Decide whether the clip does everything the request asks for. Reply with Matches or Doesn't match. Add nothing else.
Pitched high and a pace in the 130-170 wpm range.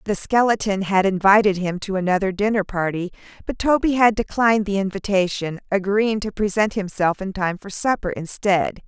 Matches